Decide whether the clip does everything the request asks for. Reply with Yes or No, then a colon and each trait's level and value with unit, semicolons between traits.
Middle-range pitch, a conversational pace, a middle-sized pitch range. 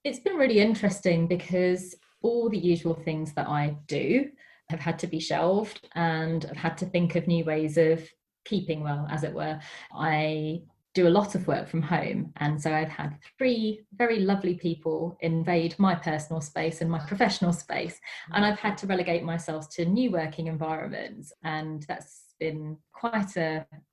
Yes: medium, 170 Hz; average, 175 wpm; average, 3.4 semitones